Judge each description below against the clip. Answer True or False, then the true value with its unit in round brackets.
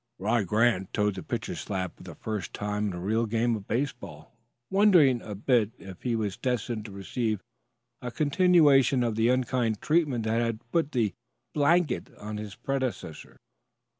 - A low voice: True (115 Hz)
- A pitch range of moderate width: True (3.9 semitones)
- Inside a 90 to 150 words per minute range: False (165 wpm)